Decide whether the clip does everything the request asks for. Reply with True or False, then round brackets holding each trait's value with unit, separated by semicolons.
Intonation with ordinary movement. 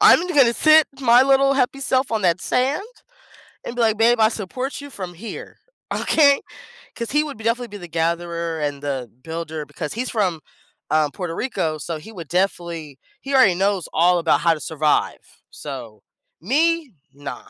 False (7.8 semitones)